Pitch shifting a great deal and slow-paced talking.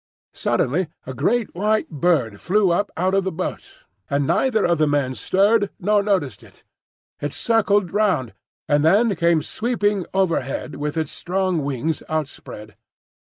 No: wide, 5.7 semitones; average, 150 wpm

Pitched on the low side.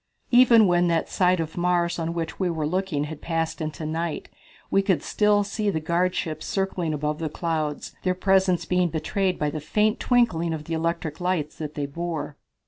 No: medium, 170 Hz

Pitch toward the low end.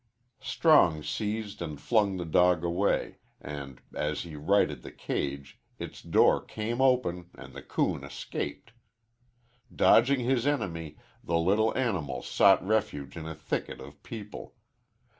Yes: very low, 90 Hz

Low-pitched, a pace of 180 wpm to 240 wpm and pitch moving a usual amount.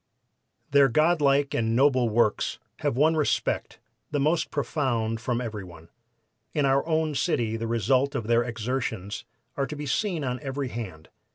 No: low, 130 Hz; average, 165 wpm; average, 4.0 semitones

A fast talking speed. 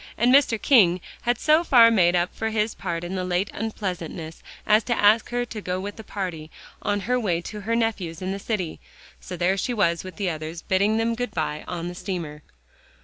Yes: fast, 215 wpm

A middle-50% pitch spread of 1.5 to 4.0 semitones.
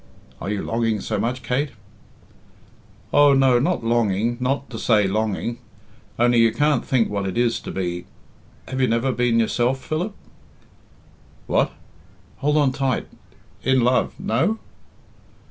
Yes: average, 2.9 semitones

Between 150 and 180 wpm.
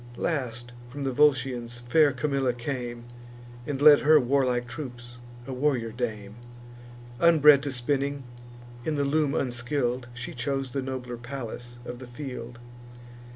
No: slow, 135 wpm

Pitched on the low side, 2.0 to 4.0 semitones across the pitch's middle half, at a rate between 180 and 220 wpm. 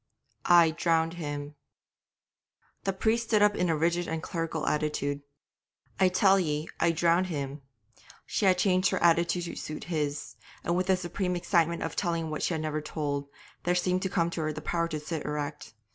No: medium, 170 Hz; average, 2.8 semitones; average, 190 wpm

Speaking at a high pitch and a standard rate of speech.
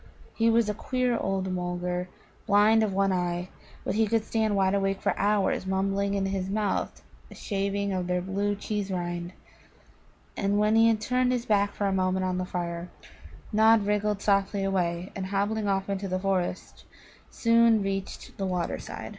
Yes: high, 195 Hz; average, 180 wpm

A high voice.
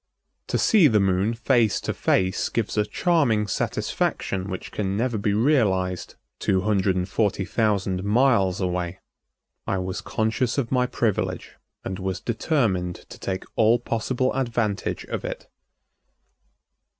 No: low, 105 Hz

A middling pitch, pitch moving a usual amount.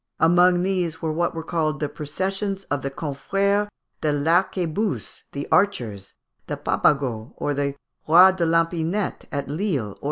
Yes: medium, 165 Hz; average, 4.7 semitones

